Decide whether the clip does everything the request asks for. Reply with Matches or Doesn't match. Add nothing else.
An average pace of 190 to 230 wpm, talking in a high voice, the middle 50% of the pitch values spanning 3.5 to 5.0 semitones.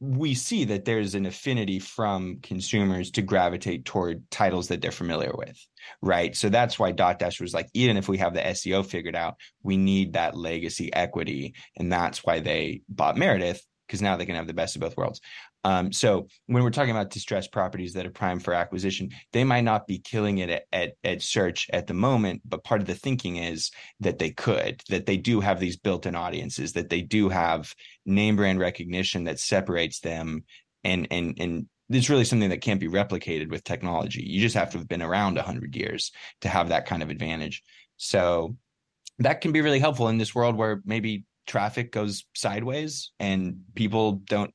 Doesn't match